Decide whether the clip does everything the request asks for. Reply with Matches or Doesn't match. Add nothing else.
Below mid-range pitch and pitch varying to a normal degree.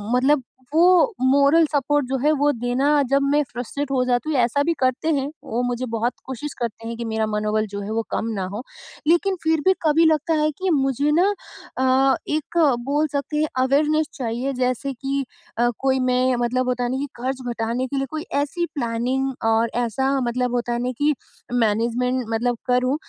Doesn't match